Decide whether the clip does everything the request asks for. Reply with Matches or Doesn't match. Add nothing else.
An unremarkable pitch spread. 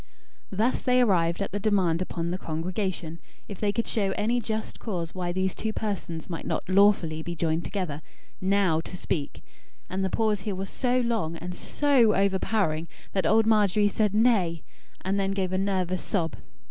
Matches